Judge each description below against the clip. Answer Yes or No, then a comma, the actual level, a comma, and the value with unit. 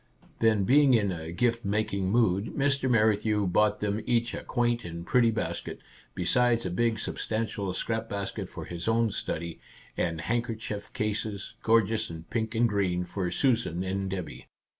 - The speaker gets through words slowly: No, average, 160 wpm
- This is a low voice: Yes, low, 105 Hz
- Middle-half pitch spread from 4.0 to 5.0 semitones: No, average, 3.6 semitones